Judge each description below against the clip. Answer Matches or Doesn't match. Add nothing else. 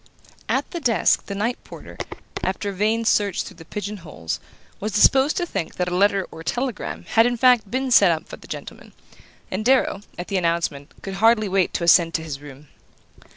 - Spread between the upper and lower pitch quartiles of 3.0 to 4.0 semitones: Doesn't match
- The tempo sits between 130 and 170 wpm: Doesn't match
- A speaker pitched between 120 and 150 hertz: Doesn't match